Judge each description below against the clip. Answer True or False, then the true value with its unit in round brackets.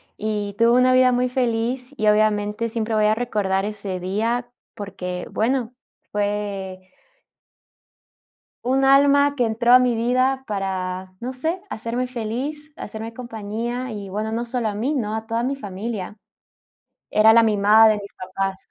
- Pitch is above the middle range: True (225 Hz)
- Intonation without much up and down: False (3.2 semitones)